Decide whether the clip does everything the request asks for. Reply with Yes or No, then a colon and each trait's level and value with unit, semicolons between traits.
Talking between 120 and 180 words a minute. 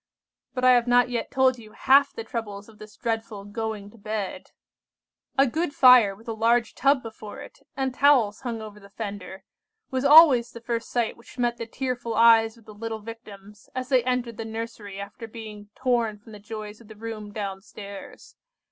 No: average, 195 wpm